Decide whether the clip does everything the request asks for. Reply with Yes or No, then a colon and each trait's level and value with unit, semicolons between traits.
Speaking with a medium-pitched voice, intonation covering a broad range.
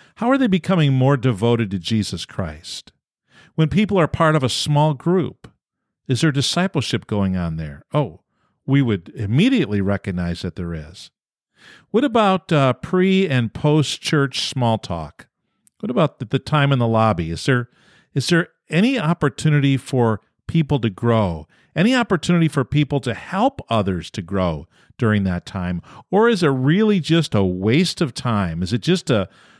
No: low, 130 Hz; wide, 7.9 semitones